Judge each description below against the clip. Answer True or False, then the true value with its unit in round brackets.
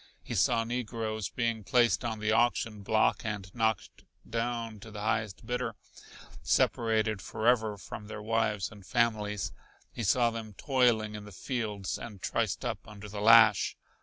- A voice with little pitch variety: True (1.9 semitones)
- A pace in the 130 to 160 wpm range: True (155 wpm)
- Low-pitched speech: True (110 Hz)